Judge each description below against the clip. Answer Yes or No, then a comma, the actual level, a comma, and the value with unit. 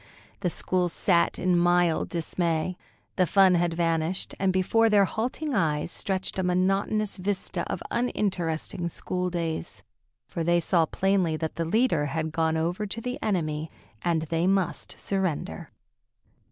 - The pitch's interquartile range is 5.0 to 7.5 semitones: No, average, 2.8 semitones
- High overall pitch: No, medium, 175 Hz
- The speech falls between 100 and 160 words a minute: Yes, average, 145 wpm